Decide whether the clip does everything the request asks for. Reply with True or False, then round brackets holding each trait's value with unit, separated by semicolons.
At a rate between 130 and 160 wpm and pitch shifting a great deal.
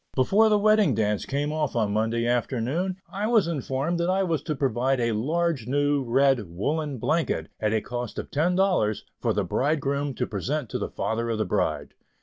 False (195 wpm; 6.1 semitones)